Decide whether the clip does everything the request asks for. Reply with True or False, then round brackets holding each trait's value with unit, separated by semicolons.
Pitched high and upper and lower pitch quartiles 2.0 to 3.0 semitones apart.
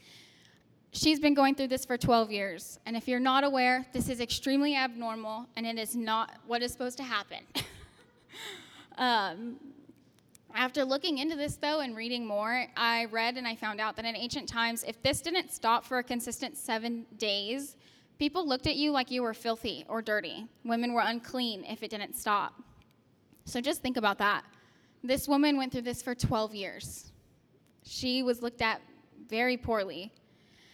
True (240 Hz; 2.7 semitones)